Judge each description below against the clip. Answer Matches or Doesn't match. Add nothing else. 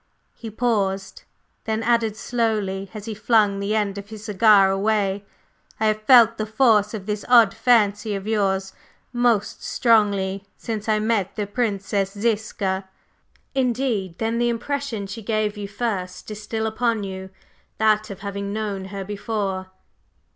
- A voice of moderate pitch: Doesn't match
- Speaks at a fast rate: Doesn't match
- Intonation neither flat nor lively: Doesn't match